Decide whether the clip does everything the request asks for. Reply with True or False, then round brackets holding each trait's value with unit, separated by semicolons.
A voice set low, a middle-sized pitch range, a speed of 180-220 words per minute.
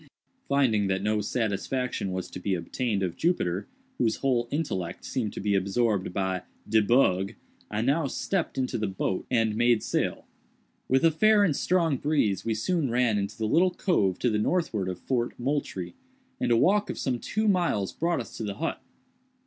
False (115 Hz; 6.3 semitones; 185 wpm)